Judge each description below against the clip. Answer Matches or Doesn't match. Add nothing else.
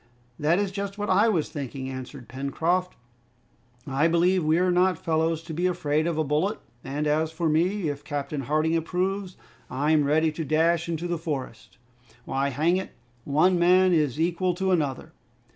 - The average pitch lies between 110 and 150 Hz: Doesn't match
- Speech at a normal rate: Matches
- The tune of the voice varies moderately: Matches